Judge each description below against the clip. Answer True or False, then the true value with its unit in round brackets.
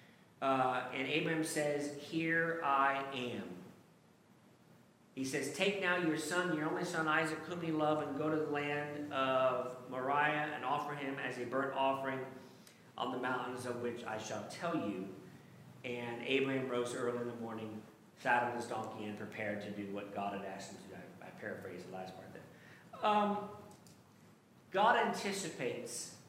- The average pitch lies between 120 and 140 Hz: True (135 Hz)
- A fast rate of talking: False (170 wpm)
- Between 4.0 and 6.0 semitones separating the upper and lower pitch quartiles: True (4.4 semitones)